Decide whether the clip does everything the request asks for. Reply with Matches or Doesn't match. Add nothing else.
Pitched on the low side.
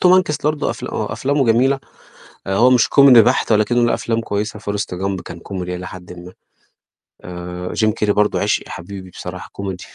Matches